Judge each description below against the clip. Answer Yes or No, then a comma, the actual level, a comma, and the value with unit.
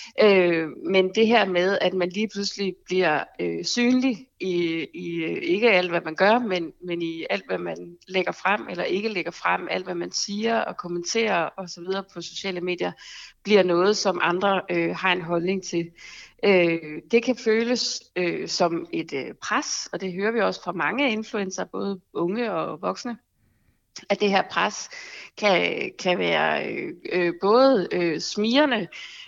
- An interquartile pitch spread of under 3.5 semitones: No, average, 4.2 semitones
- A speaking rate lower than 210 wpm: Yes, average, 170 wpm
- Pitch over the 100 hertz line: Yes, high, 190 Hz